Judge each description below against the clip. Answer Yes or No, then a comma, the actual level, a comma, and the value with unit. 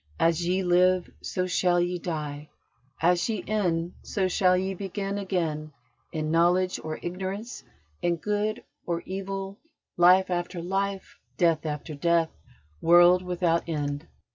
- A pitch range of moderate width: No, narrow, 2.2 semitones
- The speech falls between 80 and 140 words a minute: Yes, slow, 135 wpm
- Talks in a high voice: No, medium, 180 Hz